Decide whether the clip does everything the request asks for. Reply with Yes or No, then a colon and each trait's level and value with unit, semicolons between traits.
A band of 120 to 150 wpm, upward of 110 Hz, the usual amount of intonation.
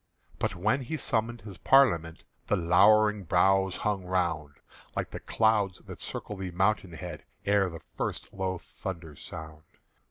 No: average, 140 wpm; very low, 95 Hz; average, 3.6 semitones